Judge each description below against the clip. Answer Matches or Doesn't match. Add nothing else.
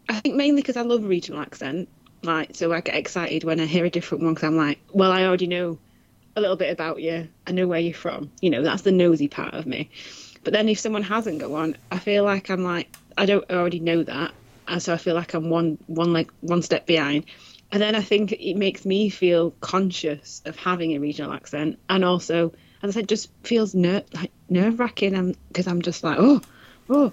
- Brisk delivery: Matches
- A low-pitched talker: Doesn't match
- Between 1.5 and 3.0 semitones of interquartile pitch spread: Doesn't match